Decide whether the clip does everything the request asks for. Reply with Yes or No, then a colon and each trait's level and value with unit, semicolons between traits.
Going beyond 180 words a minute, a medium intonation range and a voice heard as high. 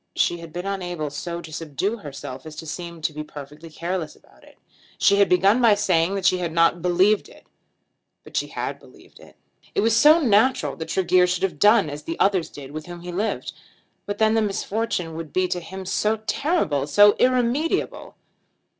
No: average, 200 wpm; average, 4.2 semitones; medium, 180 Hz